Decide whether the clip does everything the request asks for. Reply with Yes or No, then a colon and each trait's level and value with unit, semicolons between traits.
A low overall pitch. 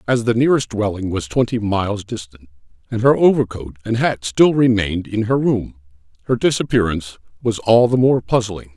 Yes: low, 110 Hz